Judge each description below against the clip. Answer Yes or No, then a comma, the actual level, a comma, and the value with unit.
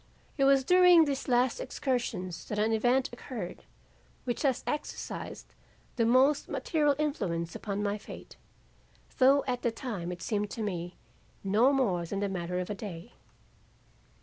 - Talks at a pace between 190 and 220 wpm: No, average, 150 wpm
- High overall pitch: Yes, high, 235 Hz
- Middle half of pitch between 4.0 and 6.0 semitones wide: Yes, wide, 5.6 semitones